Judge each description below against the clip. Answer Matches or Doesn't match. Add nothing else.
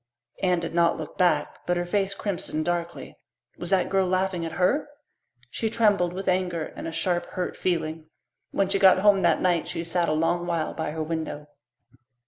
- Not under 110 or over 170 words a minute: Doesn't match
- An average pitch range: Doesn't match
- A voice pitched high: Doesn't match